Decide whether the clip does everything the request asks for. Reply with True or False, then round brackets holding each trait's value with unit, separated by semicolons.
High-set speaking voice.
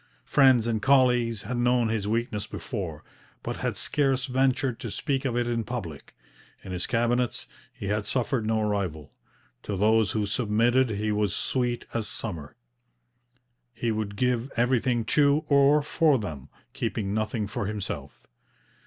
False (115 Hz)